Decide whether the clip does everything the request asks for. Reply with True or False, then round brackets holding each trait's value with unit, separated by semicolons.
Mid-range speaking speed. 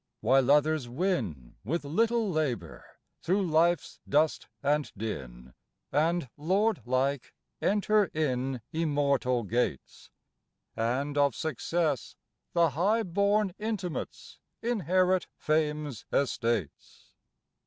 False (95 wpm)